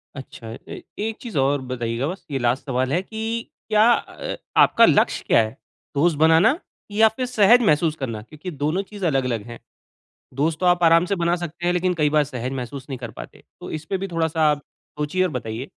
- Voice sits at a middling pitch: Yes, medium, 155 Hz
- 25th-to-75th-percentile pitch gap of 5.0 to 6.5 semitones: Yes, wide, 5.5 semitones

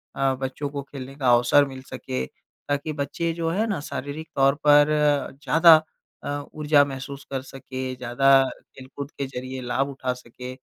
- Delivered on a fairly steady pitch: Yes, narrow, 2.0 semitones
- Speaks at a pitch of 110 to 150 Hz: Yes, low, 135 Hz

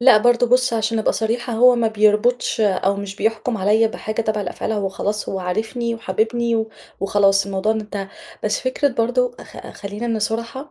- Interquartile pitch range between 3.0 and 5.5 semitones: No, narrow, 2.5 semitones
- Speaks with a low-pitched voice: No, high, 220 Hz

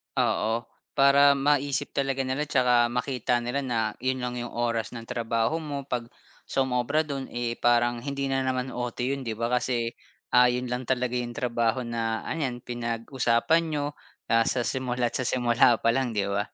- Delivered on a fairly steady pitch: Yes, narrow, 2.2 semitones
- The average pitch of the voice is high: No, low, 125 Hz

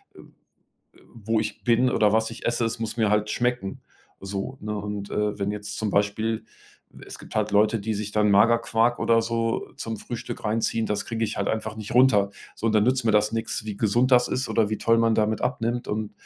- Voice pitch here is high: No, low, 110 Hz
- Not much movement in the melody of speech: Yes, narrow, 1.7 semitones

